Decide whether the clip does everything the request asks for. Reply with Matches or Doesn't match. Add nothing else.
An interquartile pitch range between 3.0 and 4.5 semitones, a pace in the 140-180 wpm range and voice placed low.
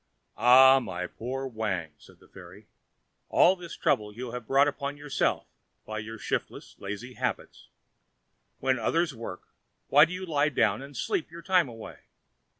Doesn't match